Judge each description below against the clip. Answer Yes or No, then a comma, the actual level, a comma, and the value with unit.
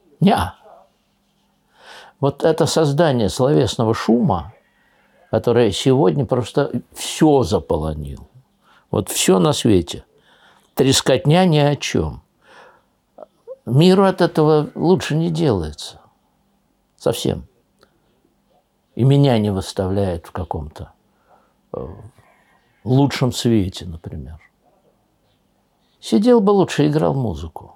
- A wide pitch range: Yes, wide, 7.5 semitones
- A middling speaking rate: No, slow, 85 wpm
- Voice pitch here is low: Yes, low, 130 Hz